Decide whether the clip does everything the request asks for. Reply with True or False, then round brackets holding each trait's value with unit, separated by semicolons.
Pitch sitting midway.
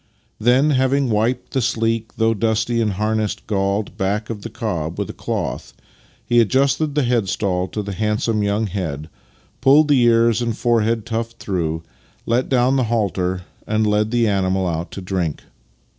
False (110 Hz)